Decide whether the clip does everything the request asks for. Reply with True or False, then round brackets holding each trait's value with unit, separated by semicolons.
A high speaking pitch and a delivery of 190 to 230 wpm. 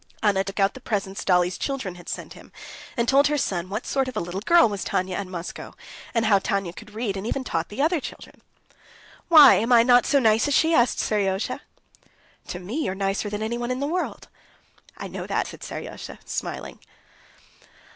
True (215 Hz; 195 wpm)